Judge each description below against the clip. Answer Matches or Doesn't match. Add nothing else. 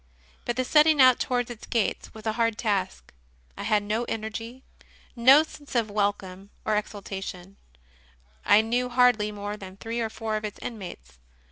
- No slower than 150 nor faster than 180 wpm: Matches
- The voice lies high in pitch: Matches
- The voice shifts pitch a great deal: Doesn't match